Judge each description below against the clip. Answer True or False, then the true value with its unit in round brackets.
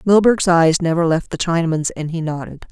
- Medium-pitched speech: True (170 Hz)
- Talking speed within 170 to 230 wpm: True (200 wpm)